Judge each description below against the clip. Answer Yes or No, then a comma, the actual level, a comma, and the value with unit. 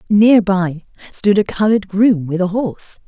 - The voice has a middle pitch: No, high, 195 Hz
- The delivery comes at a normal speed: Yes, average, 175 wpm